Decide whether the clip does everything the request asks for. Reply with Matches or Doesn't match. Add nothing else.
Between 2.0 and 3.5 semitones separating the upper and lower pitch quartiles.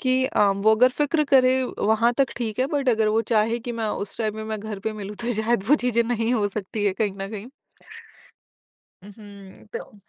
Matches